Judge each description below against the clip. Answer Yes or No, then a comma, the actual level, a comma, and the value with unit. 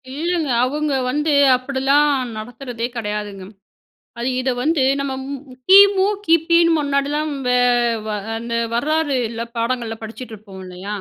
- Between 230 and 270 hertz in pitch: Yes, very high, 265 Hz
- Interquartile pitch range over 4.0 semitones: Yes, average, 4.6 semitones